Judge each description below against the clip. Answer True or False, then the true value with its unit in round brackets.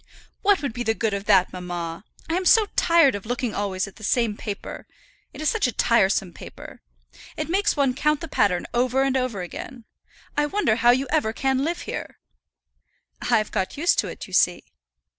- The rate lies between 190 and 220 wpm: True (200 wpm)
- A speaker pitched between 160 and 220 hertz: False (245 Hz)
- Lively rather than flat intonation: True (6.6 semitones)